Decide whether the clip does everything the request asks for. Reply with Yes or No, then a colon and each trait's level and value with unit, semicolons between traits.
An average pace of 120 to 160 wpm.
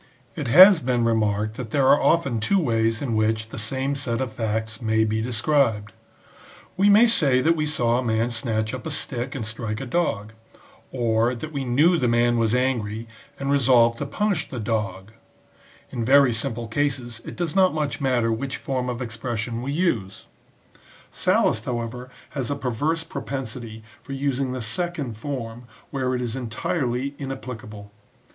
No: average, 175 wpm